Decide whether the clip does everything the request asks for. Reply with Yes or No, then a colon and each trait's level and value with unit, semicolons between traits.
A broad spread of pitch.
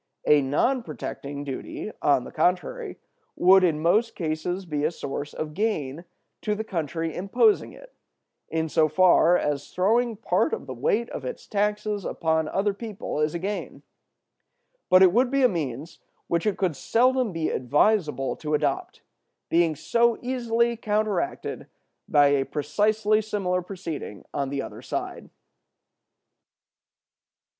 Yes: wide, 6.0 semitones